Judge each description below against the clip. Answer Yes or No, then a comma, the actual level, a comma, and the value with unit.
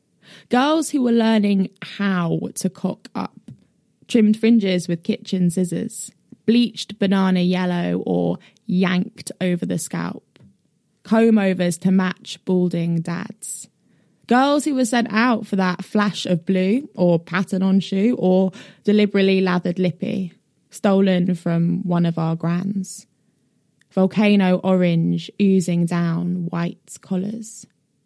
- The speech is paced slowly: Yes, slow, 120 wpm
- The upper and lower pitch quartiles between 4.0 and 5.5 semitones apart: No, average, 3.0 semitones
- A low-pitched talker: No, high, 190 Hz